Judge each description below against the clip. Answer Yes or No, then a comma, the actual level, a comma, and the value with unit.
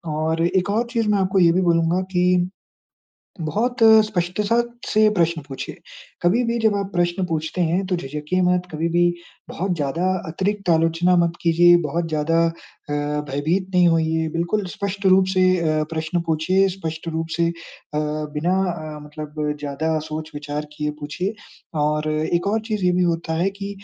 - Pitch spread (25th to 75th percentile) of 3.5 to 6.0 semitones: No, average, 2.9 semitones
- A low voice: No, medium, 170 Hz